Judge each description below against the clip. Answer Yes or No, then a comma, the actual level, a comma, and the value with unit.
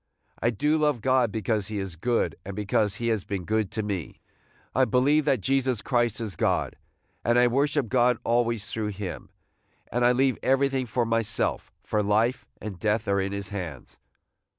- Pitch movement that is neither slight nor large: Yes, average, 3.6 semitones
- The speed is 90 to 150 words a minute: No, average, 180 wpm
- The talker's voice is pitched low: Yes, low, 115 Hz